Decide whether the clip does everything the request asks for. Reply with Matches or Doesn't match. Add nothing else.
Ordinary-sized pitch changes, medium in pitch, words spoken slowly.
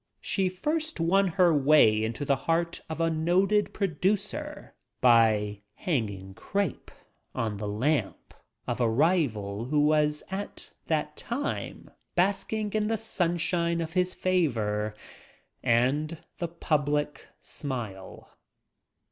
Doesn't match